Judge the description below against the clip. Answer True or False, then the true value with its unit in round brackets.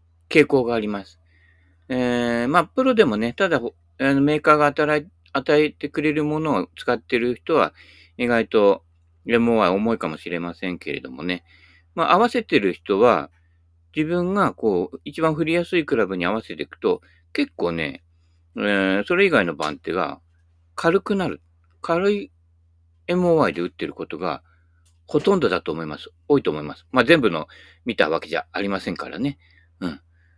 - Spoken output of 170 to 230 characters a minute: False (320 characters per minute)